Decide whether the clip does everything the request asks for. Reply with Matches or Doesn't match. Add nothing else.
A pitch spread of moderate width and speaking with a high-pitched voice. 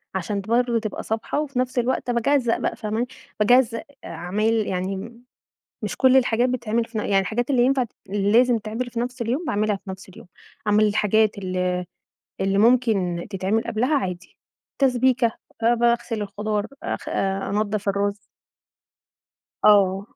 Matches